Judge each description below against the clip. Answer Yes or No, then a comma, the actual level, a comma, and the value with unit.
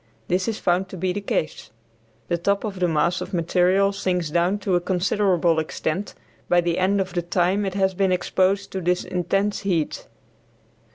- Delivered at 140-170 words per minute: No, average, 185 wpm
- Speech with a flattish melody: Yes, narrow, 2.0 semitones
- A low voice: No, medium, 185 Hz